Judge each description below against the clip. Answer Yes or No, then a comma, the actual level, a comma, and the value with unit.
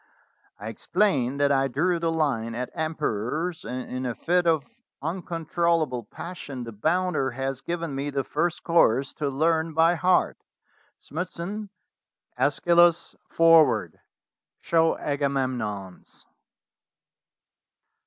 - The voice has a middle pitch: Yes, medium, 155 Hz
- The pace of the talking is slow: Yes, slow, 115 wpm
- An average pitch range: Yes, average, 4.7 semitones